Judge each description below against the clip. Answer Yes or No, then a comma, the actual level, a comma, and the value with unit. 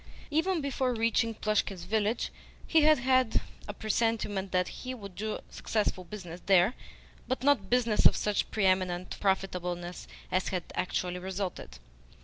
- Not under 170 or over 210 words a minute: No, average, 140 wpm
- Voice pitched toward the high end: Yes, high, 210 Hz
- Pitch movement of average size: Yes, average, 4.3 semitones